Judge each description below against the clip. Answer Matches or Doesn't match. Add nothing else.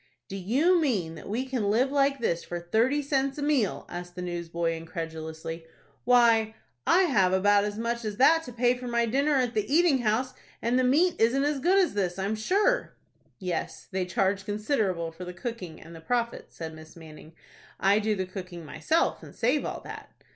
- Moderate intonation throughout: Doesn't match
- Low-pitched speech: Doesn't match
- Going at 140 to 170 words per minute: Doesn't match